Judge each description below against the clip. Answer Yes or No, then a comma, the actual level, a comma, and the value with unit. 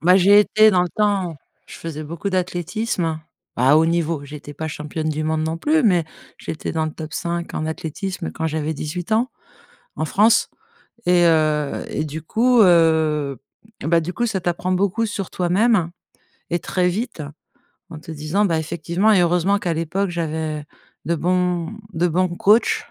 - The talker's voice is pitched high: No, medium, 170 Hz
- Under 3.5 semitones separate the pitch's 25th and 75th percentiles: Yes, average, 3.1 semitones